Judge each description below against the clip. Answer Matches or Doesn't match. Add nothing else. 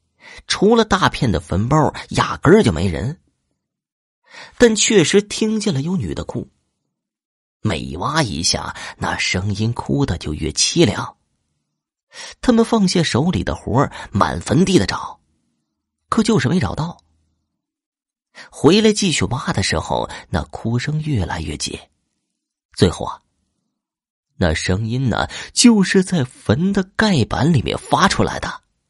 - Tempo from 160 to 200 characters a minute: Matches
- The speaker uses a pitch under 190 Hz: Matches